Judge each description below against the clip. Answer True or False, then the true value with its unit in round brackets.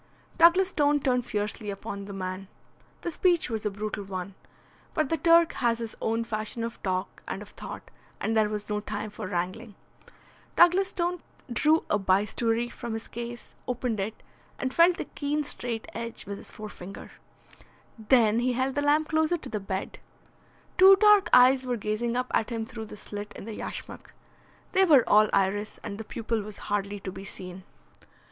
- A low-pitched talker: False (225 Hz)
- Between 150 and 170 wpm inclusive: False (180 wpm)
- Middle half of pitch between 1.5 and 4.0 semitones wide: False (4.7 semitones)